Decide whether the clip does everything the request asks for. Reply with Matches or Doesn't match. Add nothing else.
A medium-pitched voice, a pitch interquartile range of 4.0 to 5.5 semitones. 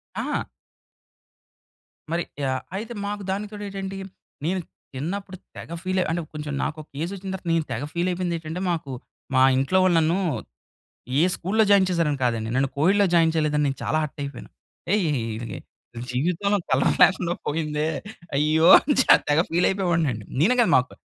Matches